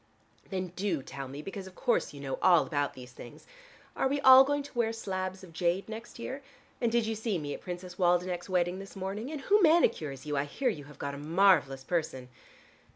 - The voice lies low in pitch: No, medium, 185 Hz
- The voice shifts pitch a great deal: Yes, wide, 7.1 semitones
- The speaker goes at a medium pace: No, fast, 220 wpm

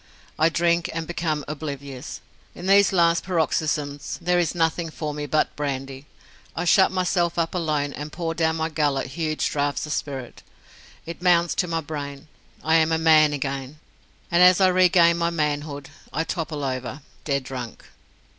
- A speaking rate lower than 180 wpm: Yes, average, 165 wpm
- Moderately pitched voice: Yes, medium, 160 Hz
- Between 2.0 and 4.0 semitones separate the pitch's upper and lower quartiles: Yes, average, 2.8 semitones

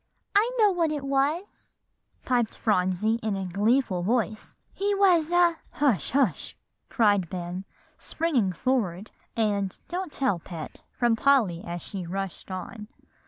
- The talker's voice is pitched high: Yes, high, 225 Hz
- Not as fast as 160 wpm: Yes, slow, 135 wpm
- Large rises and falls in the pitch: Yes, wide, 7.4 semitones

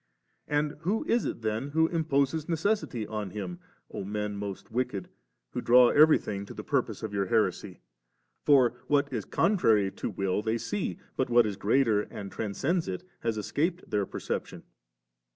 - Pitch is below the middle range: Yes, low, 120 Hz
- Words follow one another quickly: No, average, 165 wpm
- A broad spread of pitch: Yes, wide, 6.4 semitones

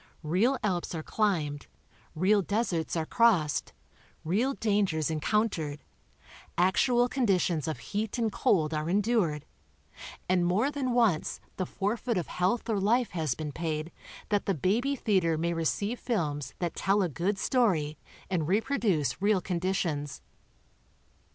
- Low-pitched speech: No, medium, 185 Hz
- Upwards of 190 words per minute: No, slow, 135 wpm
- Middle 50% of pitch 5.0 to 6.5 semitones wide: Yes, wide, 5.4 semitones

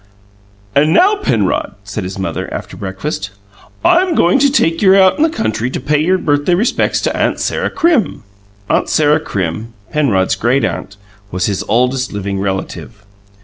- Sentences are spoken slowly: No, average, 165 wpm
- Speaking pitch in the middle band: No, low, 130 Hz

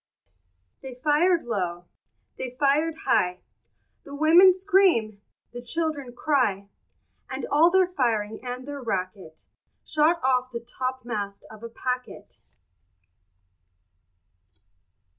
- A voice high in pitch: Yes, very high, 255 Hz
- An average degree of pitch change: No, wide, 5.9 semitones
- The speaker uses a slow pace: Yes, slow, 105 wpm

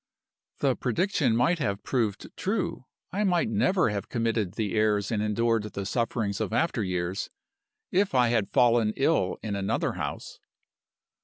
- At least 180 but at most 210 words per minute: No, average, 150 wpm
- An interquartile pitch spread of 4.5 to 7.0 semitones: Yes, average, 4.8 semitones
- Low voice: Yes, low, 115 Hz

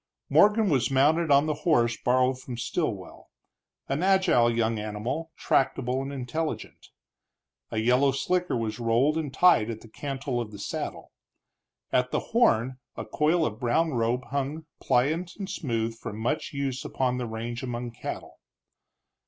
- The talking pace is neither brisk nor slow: Yes, average, 155 wpm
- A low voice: Yes, low, 130 Hz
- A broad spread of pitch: No, average, 4.5 semitones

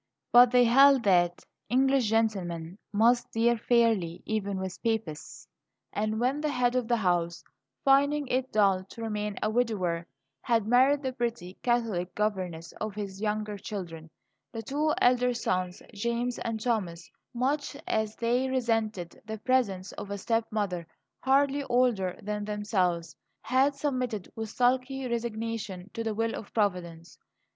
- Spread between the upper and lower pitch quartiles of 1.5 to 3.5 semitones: No, average, 4.2 semitones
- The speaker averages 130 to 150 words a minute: Yes, average, 145 wpm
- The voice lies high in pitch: Yes, high, 225 Hz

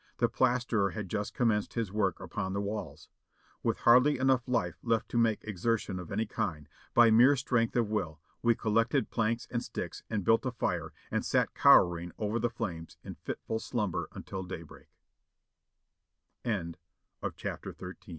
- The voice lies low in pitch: Yes, low, 110 Hz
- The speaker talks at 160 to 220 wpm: No, average, 145 wpm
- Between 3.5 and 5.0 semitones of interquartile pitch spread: No, average, 2.9 semitones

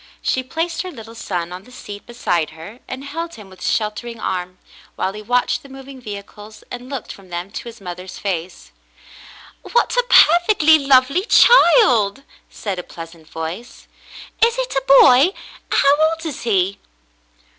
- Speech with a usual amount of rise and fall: No, wide, 6.8 semitones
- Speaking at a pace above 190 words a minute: No, average, 165 wpm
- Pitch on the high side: Yes, high, 240 Hz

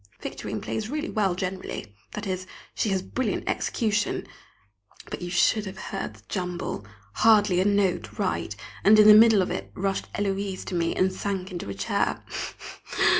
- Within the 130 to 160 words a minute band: No, average, 175 wpm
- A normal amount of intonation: No, narrow, 2.3 semitones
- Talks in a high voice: Yes, high, 195 Hz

